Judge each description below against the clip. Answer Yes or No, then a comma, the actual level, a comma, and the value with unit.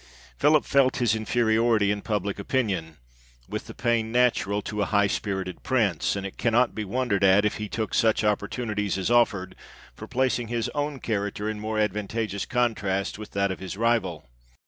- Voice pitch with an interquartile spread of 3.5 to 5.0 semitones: No, average, 2.8 semitones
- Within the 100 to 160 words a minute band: No, average, 180 wpm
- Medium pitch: No, low, 110 Hz